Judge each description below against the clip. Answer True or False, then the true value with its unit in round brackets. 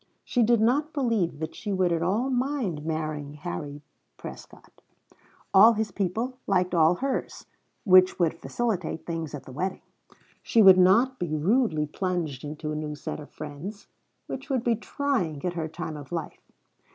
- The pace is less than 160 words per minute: False (165 wpm)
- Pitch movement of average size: False (6.6 semitones)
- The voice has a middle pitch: True (180 Hz)